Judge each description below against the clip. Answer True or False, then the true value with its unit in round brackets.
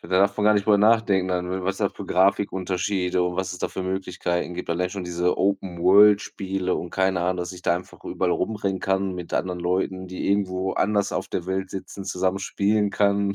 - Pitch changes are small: True (1.6 semitones)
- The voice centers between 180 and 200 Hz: False (95 Hz)